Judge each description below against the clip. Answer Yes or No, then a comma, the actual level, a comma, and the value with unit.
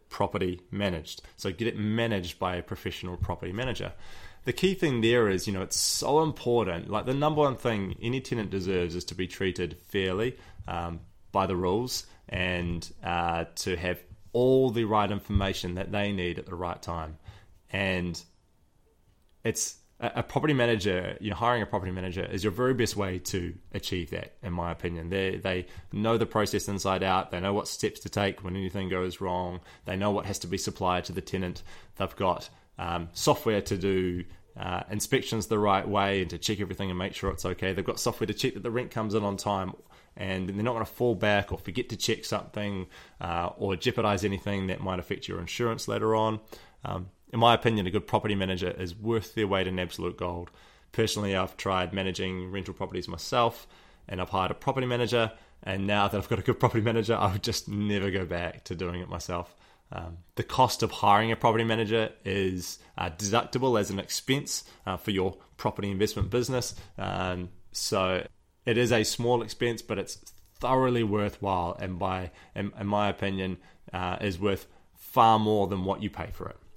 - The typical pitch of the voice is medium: No, low, 100 Hz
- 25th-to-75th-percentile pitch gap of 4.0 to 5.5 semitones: No, average, 3.2 semitones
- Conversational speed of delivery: Yes, average, 195 wpm